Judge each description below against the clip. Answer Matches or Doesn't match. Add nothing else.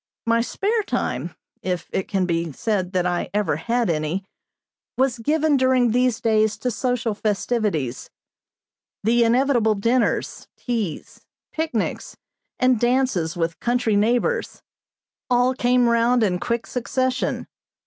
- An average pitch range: Matches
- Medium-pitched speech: Doesn't match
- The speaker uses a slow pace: Matches